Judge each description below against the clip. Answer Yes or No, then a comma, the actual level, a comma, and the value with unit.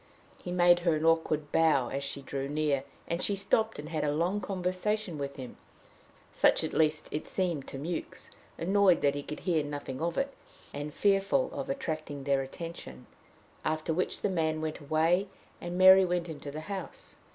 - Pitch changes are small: No, average, 3.9 semitones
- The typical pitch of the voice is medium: Yes, medium, 160 Hz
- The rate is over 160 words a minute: Yes, average, 185 wpm